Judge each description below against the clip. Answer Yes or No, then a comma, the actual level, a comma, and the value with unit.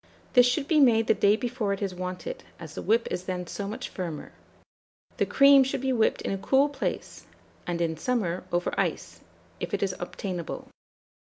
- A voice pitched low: No, high, 210 Hz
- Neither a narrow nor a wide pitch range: No, wide, 6.1 semitones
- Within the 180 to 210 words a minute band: Yes, average, 190 wpm